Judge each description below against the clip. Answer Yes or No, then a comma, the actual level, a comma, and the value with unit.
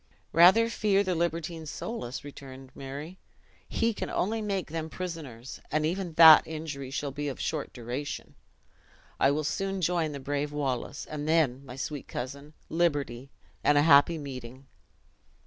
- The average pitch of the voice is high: No, medium, 150 Hz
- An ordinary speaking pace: Yes, average, 150 wpm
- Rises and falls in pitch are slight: No, average, 3.5 semitones